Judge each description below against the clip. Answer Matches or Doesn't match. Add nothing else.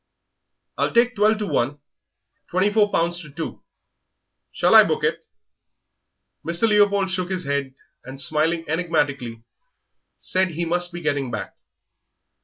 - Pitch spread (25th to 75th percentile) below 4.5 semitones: Doesn't match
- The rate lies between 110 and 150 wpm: Matches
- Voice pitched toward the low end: Doesn't match